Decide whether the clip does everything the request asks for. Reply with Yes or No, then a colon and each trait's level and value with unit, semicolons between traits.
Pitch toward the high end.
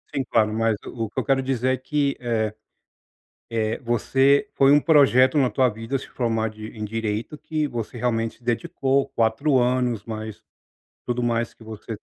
No: low, 120 Hz